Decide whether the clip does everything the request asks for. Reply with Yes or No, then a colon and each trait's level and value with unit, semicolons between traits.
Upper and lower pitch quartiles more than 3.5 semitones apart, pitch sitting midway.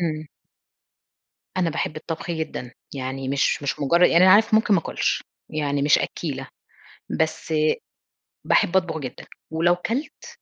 Yes: average, 4.0 semitones; medium, 160 Hz